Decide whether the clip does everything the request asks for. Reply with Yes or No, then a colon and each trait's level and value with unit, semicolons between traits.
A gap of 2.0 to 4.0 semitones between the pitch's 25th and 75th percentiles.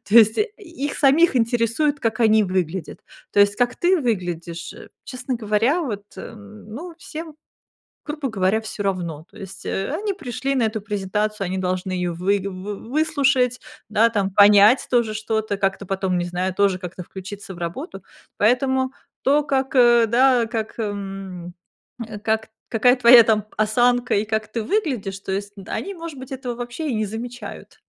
No: average, 4.6 semitones